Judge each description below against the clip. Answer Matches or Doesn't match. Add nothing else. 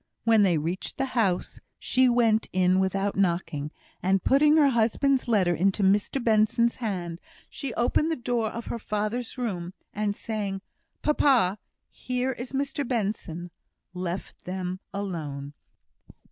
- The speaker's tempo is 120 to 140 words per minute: Matches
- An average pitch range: Matches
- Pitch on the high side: Matches